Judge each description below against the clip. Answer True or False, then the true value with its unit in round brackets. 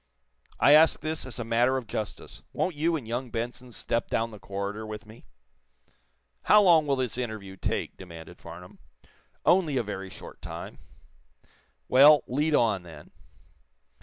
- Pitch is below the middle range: True (120 Hz)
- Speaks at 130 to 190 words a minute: True (155 wpm)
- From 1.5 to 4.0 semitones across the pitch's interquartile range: False (5.6 semitones)